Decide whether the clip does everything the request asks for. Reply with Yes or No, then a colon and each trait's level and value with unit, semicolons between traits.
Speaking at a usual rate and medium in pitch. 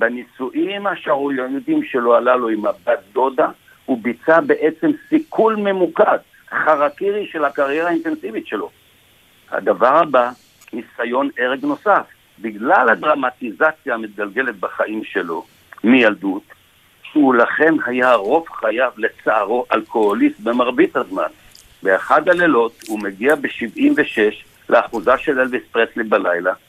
Yes: average, 110 wpm; medium, 155 Hz